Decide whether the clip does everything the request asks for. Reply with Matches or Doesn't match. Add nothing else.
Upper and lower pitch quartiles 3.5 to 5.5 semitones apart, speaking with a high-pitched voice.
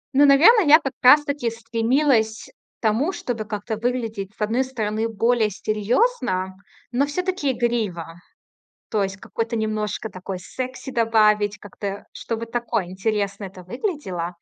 Matches